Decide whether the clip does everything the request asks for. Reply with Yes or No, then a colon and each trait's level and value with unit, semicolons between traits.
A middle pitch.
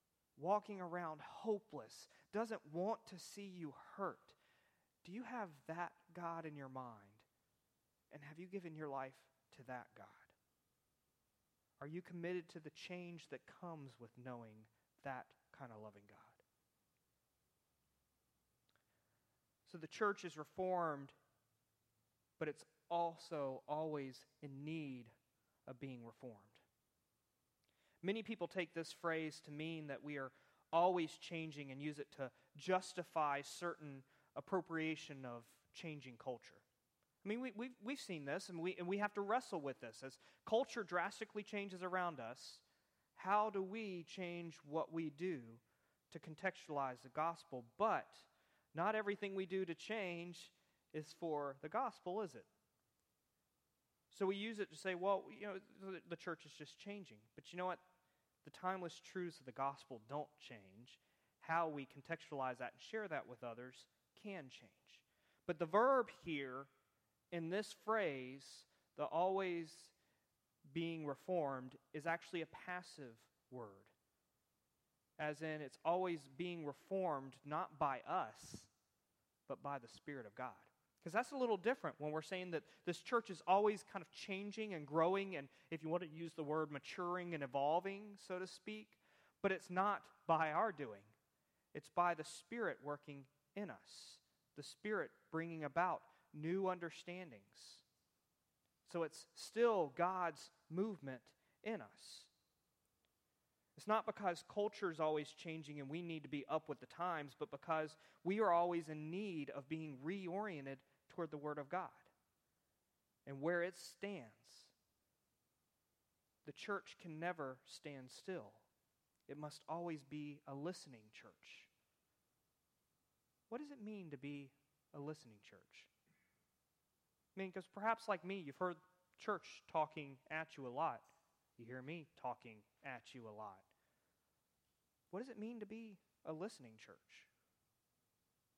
Yes: medium, 160 Hz